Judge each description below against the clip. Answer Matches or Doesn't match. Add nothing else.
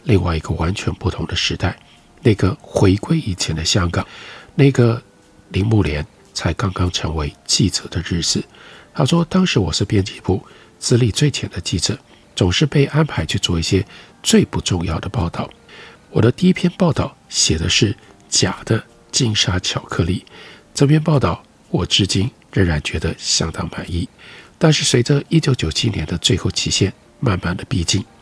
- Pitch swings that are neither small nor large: Doesn't match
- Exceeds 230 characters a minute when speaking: Matches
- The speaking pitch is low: Matches